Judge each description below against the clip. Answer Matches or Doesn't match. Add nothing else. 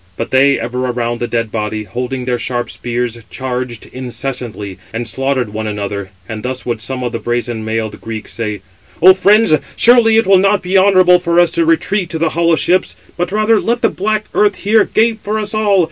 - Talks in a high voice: Doesn't match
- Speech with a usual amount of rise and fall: Doesn't match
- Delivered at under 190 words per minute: Doesn't match